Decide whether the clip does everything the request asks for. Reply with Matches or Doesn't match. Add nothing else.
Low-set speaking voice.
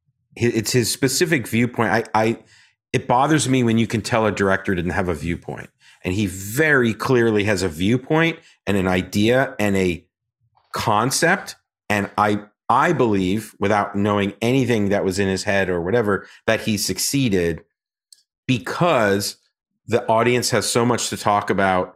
Matches